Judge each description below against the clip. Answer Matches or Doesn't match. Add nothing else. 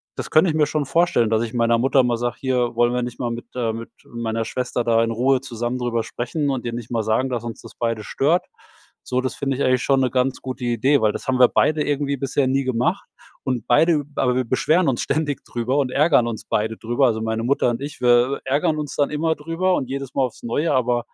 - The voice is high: Doesn't match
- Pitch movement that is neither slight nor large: Matches